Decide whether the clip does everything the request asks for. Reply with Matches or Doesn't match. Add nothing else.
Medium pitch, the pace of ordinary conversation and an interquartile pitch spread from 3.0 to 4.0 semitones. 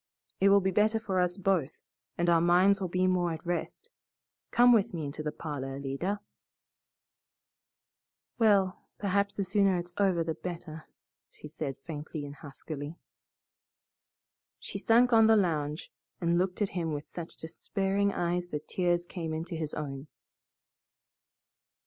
Matches